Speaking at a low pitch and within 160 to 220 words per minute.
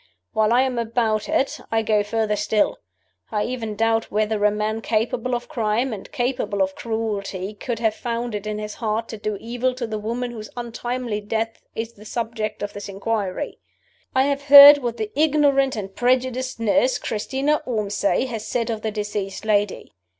No: high, 225 Hz; average, 180 wpm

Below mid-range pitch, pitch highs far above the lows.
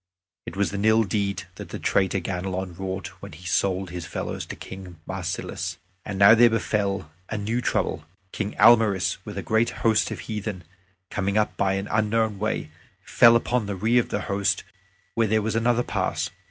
No: low, 100 Hz; average, 2.7 semitones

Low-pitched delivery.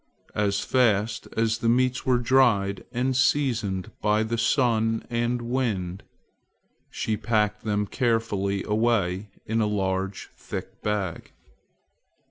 Yes: low, 110 Hz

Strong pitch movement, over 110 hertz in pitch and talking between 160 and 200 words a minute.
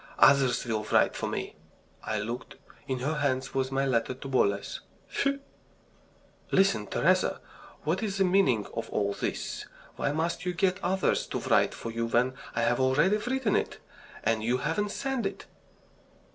Yes: wide, 8.4 semitones; low, 135 Hz; average, 165 wpm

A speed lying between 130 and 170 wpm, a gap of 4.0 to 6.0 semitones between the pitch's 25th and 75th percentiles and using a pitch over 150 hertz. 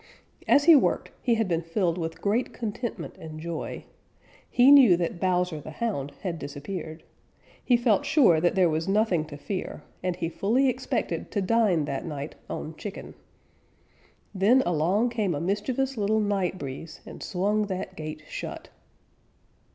Yes: average, 160 wpm; average, 5.1 semitones; medium, 185 Hz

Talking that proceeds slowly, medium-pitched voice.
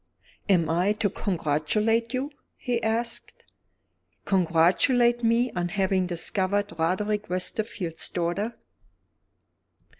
No: slow, 90 wpm; high, 200 Hz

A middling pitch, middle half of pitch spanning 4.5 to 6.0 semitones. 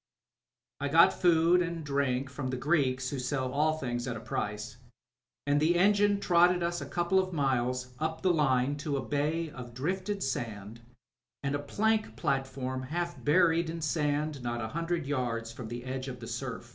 Yes: medium, 145 Hz; average, 4.8 semitones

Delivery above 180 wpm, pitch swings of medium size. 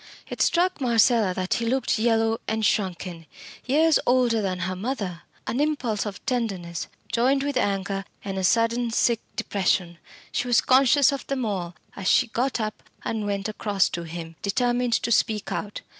No: average, 170 wpm; average, 4.3 semitones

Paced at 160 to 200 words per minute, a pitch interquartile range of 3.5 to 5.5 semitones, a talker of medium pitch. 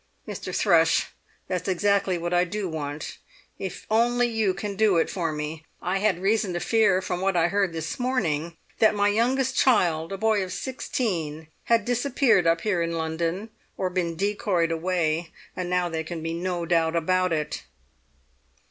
Yes: average, 175 wpm; average, 3.9 semitones; medium, 180 Hz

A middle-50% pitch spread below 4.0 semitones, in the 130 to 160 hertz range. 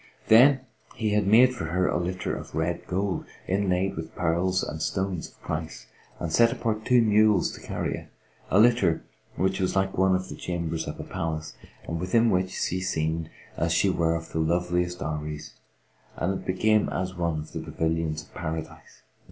No: average, 3.2 semitones; very low, 90 Hz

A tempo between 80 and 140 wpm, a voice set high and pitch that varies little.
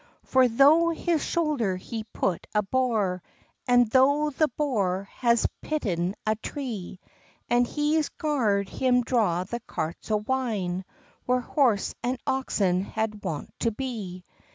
No: slow, 135 wpm; high, 235 Hz; average, 5.0 semitones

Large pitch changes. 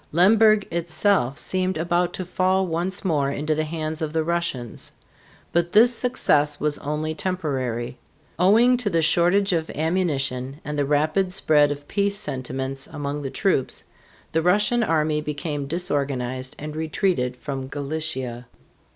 No: average, 4.3 semitones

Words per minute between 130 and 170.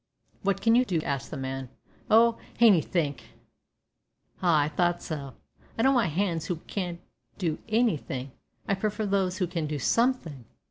Yes: average, 155 wpm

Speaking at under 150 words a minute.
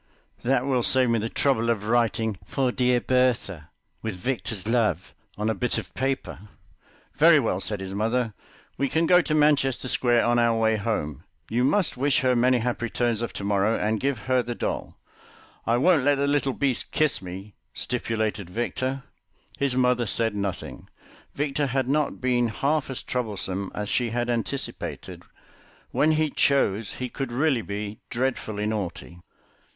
No: average, 165 wpm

